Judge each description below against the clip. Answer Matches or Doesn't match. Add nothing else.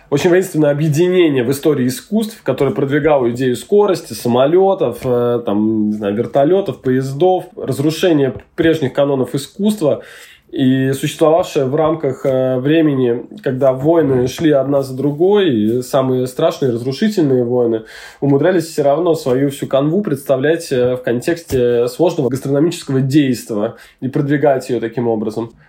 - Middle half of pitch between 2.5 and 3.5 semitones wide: Doesn't match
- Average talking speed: Matches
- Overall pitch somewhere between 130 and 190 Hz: Matches